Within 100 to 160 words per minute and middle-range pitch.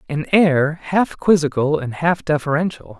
Yes: average, 140 wpm; medium, 155 Hz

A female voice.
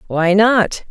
Yes: female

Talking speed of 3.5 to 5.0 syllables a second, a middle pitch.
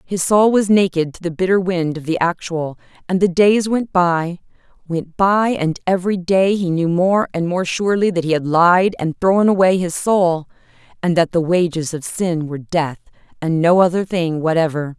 Yes: 4.8 syllables/s; medium, 175 Hz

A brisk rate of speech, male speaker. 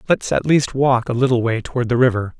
Yes: fast, 250 wpm; male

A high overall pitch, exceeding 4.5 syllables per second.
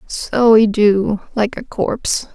No: high, 215 Hz; 3.4 syllables/s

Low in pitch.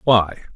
Yes: low, 100 Hz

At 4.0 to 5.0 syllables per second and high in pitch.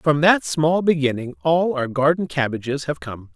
No: 4.7 syllables/s; medium, 145 Hz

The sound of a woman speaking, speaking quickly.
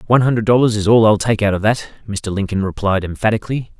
No: male; fast, 220 wpm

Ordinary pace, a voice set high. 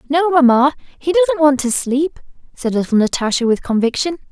Yes: average, 165 wpm; very high, 285 Hz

